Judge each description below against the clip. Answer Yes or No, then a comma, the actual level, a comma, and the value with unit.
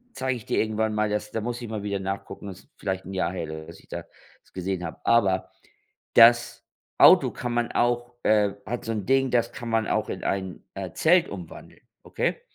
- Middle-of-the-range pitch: No, low, 105 Hz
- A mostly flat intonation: No, average, 3.8 semitones